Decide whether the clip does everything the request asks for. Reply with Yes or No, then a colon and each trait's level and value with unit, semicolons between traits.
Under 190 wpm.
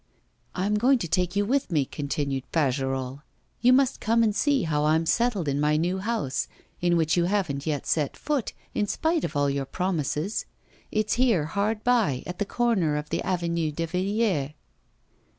Yes: average, 180 wpm